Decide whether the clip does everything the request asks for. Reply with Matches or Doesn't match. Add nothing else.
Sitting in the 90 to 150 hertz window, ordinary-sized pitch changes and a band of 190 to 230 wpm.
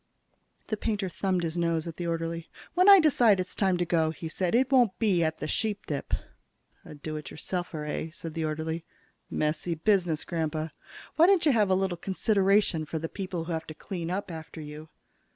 Doesn't match